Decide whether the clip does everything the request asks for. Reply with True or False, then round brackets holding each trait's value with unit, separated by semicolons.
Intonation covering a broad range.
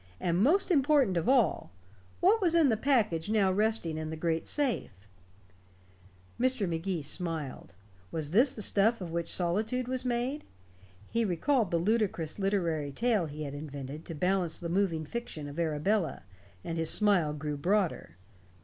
True (6.4 semitones)